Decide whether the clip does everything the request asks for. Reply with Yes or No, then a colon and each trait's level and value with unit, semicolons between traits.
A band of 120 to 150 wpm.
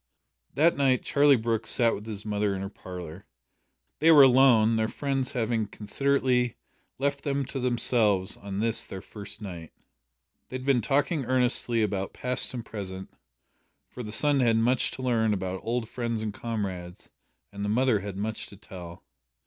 No: average, 170 wpm